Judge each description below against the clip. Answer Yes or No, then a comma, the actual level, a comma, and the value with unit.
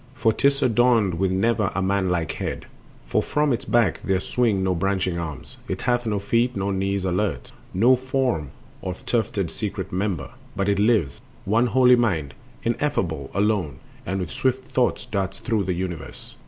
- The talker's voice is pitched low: Yes, low, 100 Hz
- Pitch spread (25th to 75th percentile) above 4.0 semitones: Yes, average, 4.4 semitones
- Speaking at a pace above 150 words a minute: Yes, average, 170 wpm